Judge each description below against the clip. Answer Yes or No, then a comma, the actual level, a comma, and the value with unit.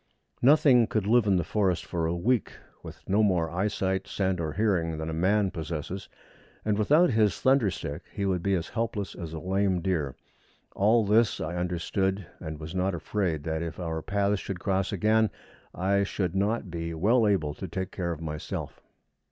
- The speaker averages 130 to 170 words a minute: No, average, 185 wpm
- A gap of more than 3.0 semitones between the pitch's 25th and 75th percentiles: Yes, average, 3.8 semitones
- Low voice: Yes, very low, 95 Hz